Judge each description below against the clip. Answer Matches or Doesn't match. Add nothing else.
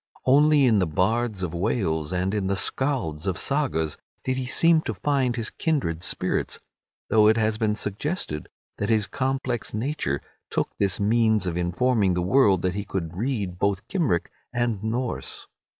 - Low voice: Matches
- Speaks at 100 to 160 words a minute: Doesn't match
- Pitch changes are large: Matches